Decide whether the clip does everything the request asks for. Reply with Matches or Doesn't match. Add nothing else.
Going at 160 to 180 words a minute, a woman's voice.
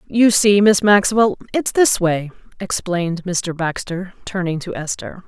Doesn't match